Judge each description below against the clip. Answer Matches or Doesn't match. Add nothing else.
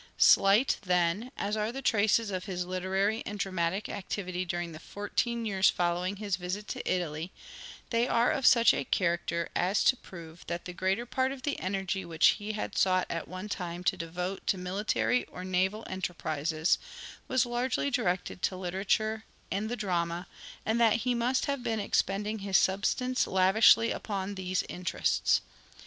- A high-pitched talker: Matches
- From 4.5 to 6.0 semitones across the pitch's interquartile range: Doesn't match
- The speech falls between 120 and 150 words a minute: Doesn't match